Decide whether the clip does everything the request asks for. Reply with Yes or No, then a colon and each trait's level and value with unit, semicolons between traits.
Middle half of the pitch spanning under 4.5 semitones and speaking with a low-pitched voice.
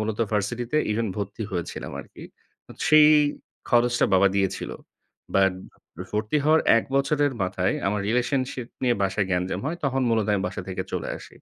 No: average, 4.9 semitones; low, 110 Hz